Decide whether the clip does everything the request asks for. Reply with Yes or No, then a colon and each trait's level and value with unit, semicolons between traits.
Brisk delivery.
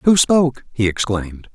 No: average, 155 wpm